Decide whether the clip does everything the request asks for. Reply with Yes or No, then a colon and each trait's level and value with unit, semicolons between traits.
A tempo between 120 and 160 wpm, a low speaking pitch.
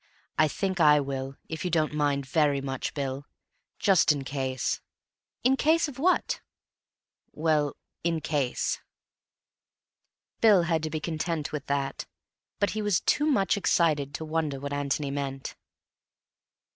No: average, 140 wpm; medium, 150 Hz